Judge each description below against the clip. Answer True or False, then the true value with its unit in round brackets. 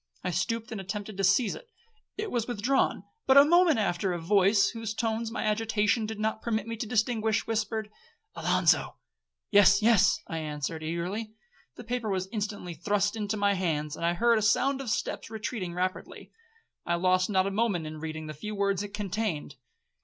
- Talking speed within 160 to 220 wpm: True (180 wpm)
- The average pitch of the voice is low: False (205 Hz)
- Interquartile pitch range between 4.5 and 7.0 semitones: False (3.7 semitones)